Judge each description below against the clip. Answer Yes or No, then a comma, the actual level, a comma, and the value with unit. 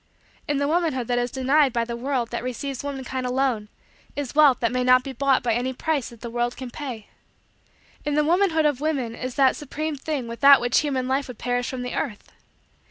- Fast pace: Yes, fast, 215 wpm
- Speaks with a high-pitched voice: Yes, very high, 260 Hz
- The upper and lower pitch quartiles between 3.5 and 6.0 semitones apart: No, average, 2.9 semitones